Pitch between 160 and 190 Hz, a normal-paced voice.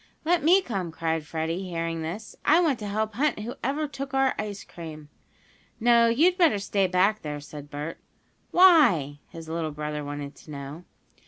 Yes: medium, 185 Hz; average, 170 wpm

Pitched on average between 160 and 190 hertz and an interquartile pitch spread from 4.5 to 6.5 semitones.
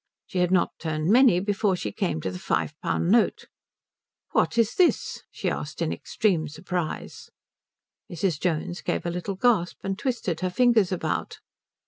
No: medium, 185 Hz; average, 4.0 semitones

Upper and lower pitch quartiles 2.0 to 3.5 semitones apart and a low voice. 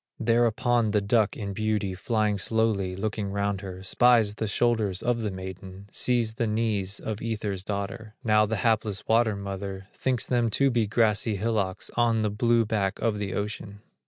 Yes: narrow, 2.4 semitones; low, 105 Hz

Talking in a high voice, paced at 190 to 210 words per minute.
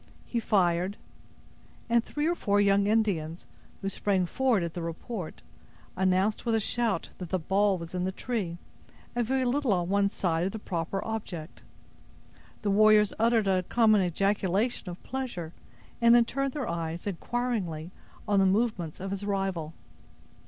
No: high, 200 Hz; average, 160 wpm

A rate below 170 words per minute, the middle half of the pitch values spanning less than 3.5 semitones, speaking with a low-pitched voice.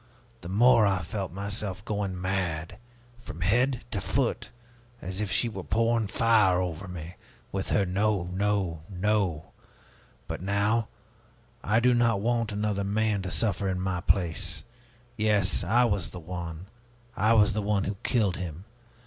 Yes: average, 155 wpm; average, 2.8 semitones; low, 100 Hz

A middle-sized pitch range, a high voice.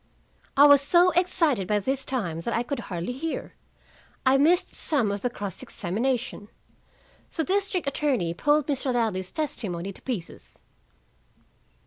No: wide, 6.7 semitones; very high, 260 Hz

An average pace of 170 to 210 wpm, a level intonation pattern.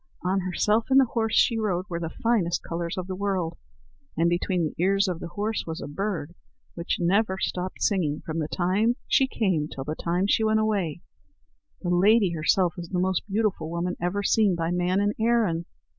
No: average, 190 wpm; average, 3.5 semitones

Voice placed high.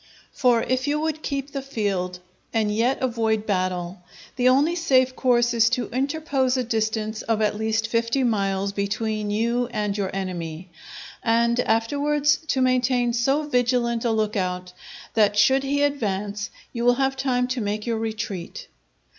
Yes: high, 230 Hz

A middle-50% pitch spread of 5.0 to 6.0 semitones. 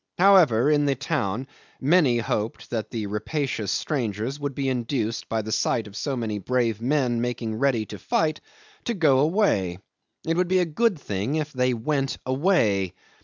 Yes: wide, 5.4 semitones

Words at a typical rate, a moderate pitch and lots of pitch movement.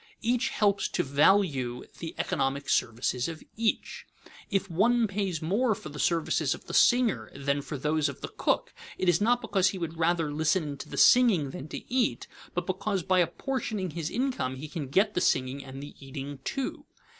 Yes: average, 190 wpm; medium, 170 Hz; wide, 6.3 semitones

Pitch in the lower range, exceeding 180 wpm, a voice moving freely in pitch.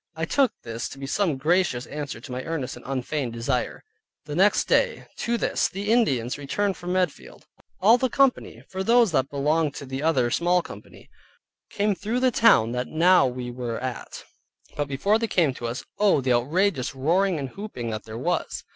No: medium, 150 Hz; average, 195 wpm; wide, 7.6 semitones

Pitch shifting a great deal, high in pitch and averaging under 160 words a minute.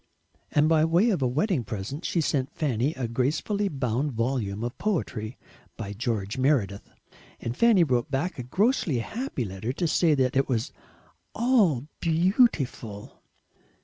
No: wide, 6.3 semitones; low, 135 Hz; average, 145 wpm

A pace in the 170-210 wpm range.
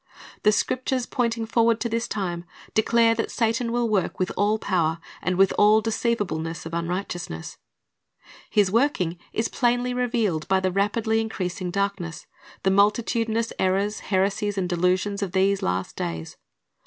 No: average, 145 wpm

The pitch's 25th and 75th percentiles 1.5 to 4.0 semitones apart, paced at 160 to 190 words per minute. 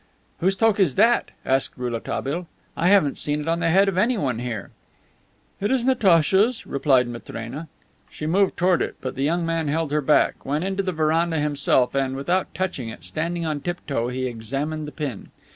No: average, 5.2 semitones; average, 185 wpm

